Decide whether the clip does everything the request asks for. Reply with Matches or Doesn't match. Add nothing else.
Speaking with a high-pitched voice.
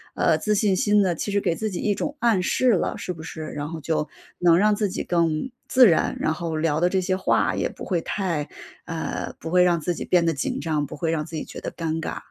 Doesn't match